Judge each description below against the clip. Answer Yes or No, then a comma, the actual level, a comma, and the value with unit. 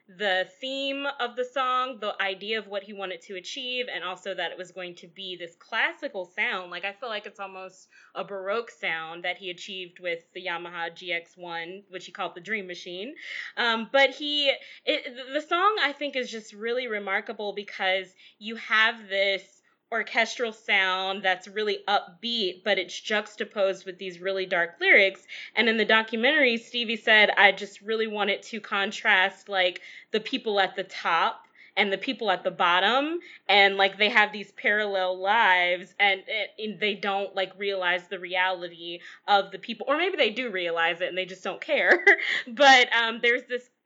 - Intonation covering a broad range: No, average, 3.7 semitones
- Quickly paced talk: No, average, 180 wpm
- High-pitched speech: Yes, high, 200 Hz